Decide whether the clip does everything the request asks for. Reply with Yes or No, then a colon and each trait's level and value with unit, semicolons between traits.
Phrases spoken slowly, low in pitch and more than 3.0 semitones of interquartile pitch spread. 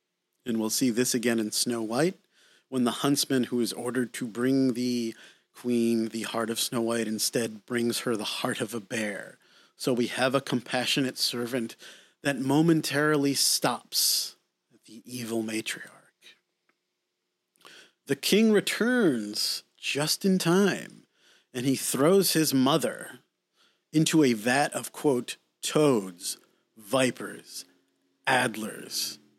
Yes: slow, 130 wpm; low, 125 Hz; average, 3.5 semitones